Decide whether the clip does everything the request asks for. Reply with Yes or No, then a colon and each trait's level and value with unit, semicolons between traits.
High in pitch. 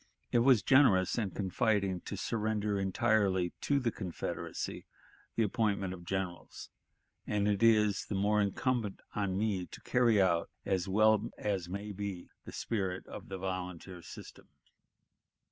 No: low, 100 Hz